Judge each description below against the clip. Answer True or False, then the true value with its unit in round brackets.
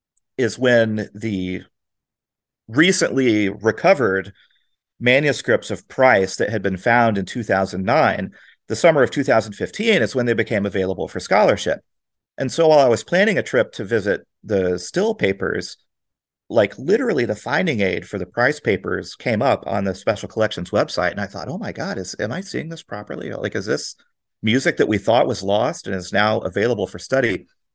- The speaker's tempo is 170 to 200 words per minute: True (175 wpm)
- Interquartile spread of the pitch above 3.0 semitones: True (3.8 semitones)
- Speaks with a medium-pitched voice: False (105 Hz)